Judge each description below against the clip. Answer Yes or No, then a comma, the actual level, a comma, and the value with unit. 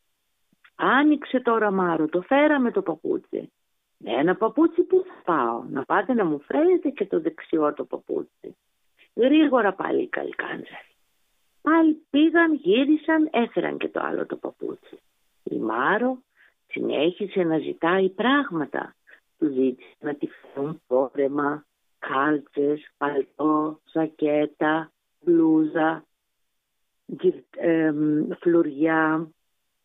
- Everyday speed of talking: No, slow, 110 wpm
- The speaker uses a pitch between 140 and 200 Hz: Yes, high, 190 Hz